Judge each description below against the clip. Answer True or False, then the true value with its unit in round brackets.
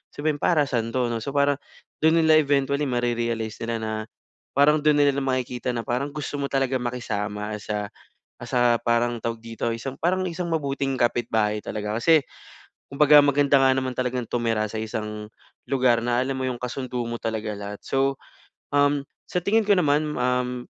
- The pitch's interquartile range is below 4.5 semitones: True (3.6 semitones)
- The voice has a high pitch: False (125 Hz)